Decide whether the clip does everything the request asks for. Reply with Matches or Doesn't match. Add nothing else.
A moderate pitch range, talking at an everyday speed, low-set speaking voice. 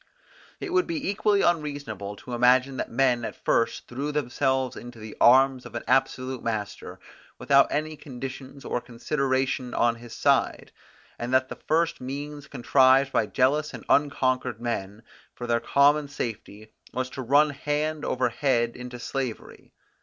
Matches